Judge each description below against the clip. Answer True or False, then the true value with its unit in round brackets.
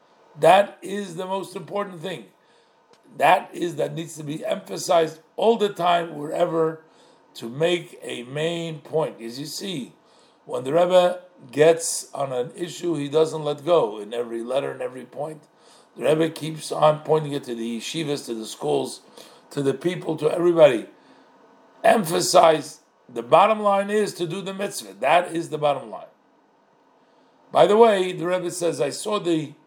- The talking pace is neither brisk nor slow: True (165 wpm)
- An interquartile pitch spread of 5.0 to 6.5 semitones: False (3.2 semitones)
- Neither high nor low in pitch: True (165 Hz)